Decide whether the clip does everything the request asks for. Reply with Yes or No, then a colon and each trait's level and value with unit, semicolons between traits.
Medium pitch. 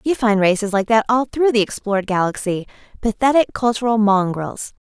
No: high, 215 Hz